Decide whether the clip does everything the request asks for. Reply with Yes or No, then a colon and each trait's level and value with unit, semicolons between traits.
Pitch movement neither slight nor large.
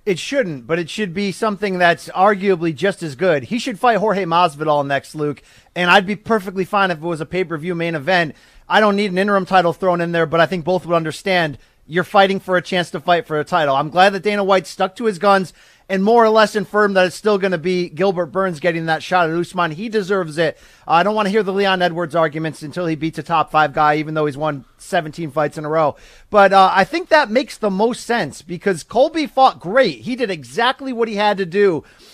Yes: average, 3.9 semitones